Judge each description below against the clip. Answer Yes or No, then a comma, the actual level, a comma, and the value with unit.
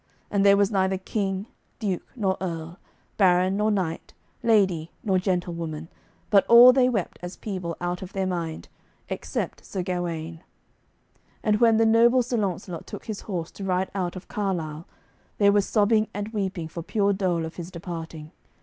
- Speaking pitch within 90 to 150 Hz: No, high, 190 Hz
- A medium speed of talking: Yes, average, 170 wpm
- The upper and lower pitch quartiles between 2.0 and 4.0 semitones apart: Yes, average, 3.2 semitones